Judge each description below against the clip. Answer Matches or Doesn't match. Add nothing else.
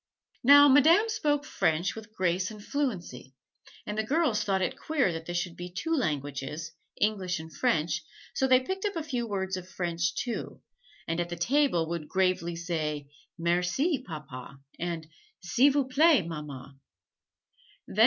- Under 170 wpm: Matches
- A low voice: Doesn't match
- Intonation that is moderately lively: Doesn't match